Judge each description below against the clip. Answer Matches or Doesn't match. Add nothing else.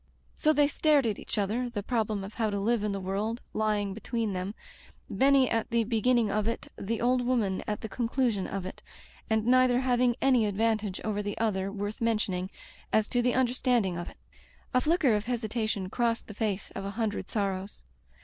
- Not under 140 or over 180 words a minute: Doesn't match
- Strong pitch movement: Doesn't match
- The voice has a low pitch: Doesn't match